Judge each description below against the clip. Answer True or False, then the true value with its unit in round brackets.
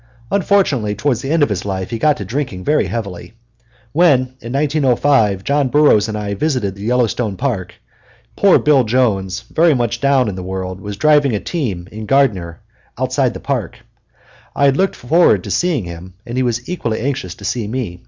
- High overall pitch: False (120 Hz)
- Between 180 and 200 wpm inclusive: True (190 wpm)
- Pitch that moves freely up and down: True (5.8 semitones)